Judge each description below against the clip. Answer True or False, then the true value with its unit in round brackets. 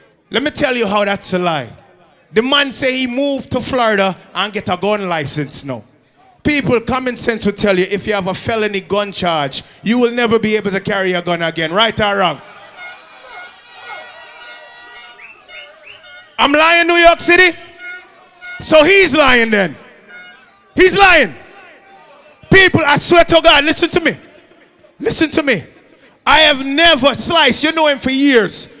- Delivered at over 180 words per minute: False (165 wpm)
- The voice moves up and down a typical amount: False (7.8 semitones)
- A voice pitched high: True (230 Hz)